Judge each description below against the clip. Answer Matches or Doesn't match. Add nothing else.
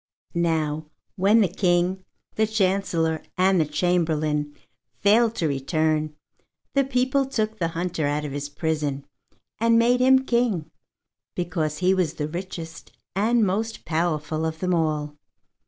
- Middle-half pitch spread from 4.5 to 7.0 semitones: Matches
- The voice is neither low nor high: Matches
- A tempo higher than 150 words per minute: Doesn't match